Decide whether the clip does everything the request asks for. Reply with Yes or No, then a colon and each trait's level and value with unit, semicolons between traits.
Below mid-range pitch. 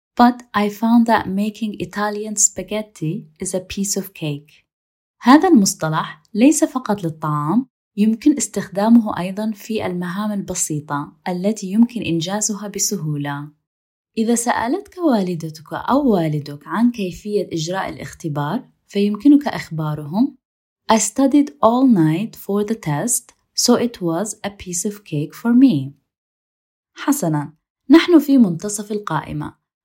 No: high, 205 Hz